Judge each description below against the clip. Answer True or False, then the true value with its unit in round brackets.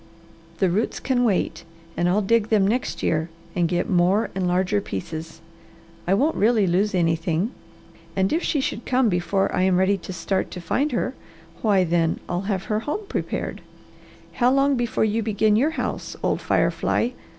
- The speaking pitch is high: True (195 Hz)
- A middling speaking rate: True (180 wpm)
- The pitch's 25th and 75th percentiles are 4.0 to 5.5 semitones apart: True (4.5 semitones)